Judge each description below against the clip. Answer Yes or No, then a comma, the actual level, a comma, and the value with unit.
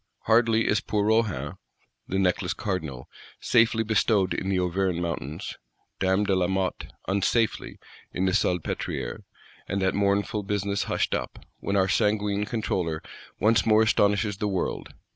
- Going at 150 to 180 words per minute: No, average, 140 wpm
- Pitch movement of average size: No, narrow, 2.3 semitones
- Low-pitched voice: Yes, low, 100 Hz